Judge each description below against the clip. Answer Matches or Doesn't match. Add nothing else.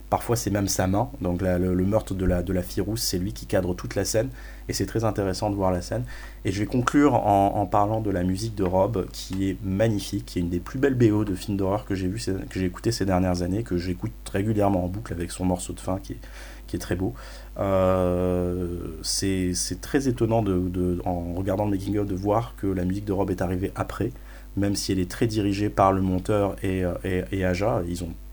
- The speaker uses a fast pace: Matches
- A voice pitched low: Matches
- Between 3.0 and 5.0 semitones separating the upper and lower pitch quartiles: Doesn't match